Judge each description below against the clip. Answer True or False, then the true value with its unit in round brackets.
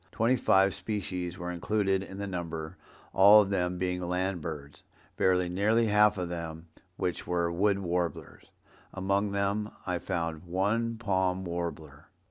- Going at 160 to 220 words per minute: False (140 wpm)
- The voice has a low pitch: True (95 Hz)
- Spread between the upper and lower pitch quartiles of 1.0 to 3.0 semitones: True (2.4 semitones)